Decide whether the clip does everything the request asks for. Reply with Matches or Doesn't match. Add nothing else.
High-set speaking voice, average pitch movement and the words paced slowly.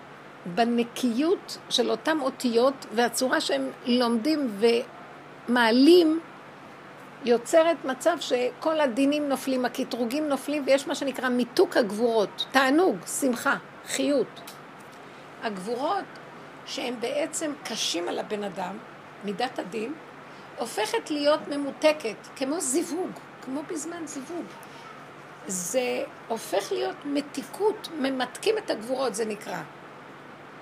Matches